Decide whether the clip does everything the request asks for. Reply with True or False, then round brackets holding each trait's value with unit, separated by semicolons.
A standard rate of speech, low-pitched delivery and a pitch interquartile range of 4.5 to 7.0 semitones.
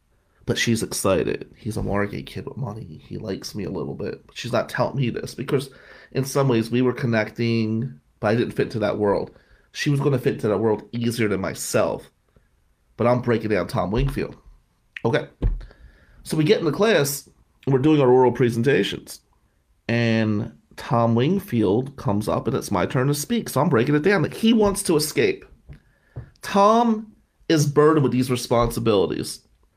True (185 wpm; 120 Hz; 5.2 semitones)